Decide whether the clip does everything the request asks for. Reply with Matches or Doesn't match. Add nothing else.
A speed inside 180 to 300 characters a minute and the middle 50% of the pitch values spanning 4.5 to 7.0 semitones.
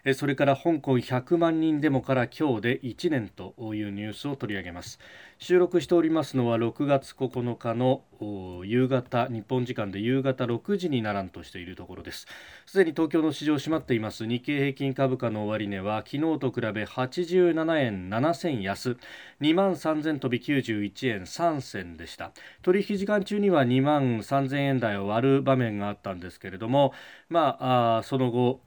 Matches